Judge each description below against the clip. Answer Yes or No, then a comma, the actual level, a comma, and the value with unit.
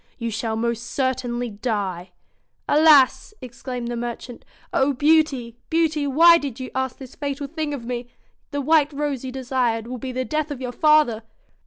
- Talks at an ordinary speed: Yes, average, 175 wpm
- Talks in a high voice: Yes, very high, 260 Hz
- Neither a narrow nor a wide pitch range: Yes, average, 3.4 semitones